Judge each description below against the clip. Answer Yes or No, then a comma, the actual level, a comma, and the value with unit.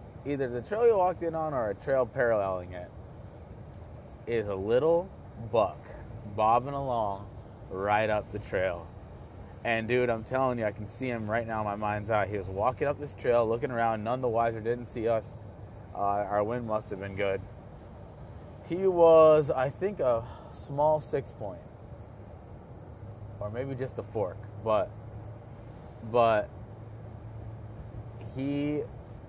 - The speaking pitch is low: Yes, low, 115 Hz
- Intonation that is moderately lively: Yes, average, 3.1 semitones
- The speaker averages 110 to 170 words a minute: Yes, average, 150 wpm